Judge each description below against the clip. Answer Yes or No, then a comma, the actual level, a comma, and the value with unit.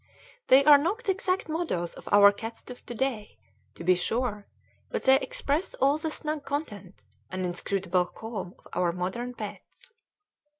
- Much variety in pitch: Yes, wide, 7.5 semitones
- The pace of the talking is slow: No, average, 160 wpm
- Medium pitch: No, high, 235 Hz